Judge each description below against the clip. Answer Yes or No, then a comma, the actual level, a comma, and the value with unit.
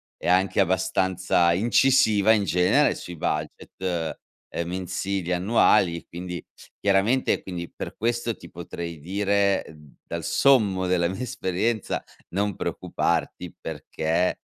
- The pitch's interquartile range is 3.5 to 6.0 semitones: No, average, 2.7 semitones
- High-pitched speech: No, very low, 95 Hz